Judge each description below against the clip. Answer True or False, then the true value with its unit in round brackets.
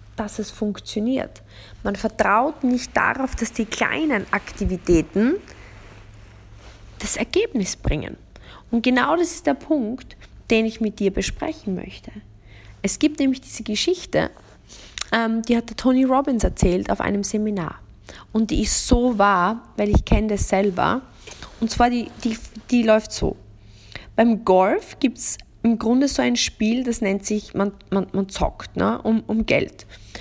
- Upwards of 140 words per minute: True (155 wpm)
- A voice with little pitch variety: False (4.8 semitones)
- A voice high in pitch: True (220 Hz)